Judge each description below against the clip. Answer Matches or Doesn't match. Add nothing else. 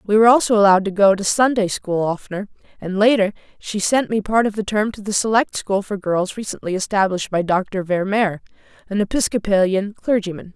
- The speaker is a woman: Matches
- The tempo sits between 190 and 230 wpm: Matches